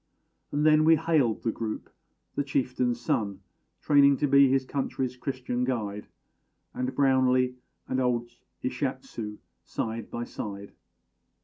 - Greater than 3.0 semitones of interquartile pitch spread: No, average, 2.7 semitones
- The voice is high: No, low, 125 Hz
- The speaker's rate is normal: No, slow, 125 wpm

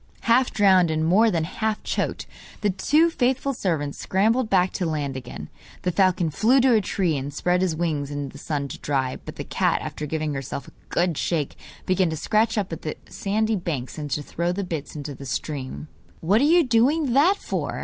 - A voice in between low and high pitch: Yes, medium, 180 Hz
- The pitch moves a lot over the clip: Yes, wide, 6.5 semitones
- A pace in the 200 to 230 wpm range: Yes, fast, 205 wpm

